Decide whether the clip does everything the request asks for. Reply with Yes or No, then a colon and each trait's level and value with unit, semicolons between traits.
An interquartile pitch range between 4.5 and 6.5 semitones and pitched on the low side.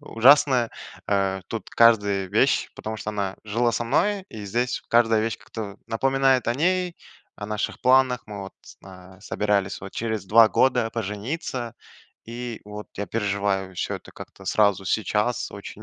No: average, 3.3 semitones; low, 110 Hz